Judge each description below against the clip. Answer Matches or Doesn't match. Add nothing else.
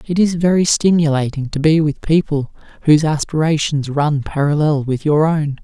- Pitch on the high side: Doesn't match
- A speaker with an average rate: Matches